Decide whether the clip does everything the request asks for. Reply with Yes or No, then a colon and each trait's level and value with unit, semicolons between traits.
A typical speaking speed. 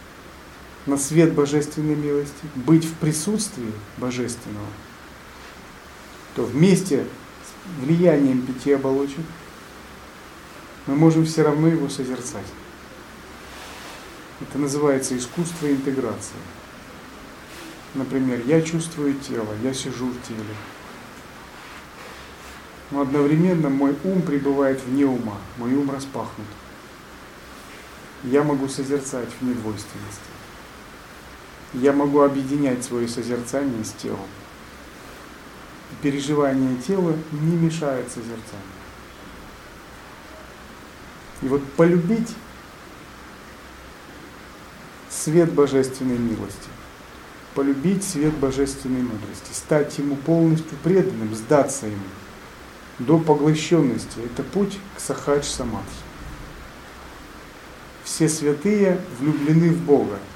No: slow, 85 wpm